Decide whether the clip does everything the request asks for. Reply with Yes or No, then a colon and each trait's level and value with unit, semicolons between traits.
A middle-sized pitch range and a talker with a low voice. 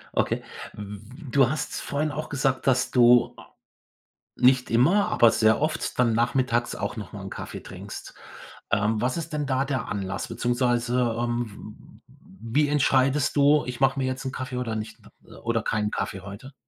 Yes: average, 3.0 semitones; low, 125 Hz